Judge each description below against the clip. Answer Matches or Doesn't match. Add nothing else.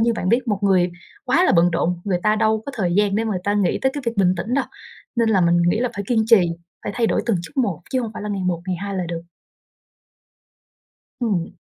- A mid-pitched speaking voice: Doesn't match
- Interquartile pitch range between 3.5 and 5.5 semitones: Matches